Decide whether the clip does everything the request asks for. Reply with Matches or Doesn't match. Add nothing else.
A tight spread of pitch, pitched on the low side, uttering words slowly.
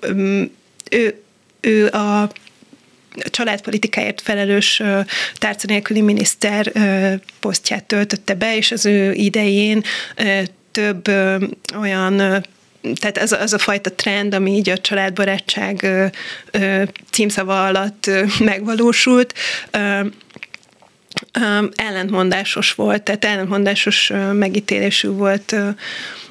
Doesn't match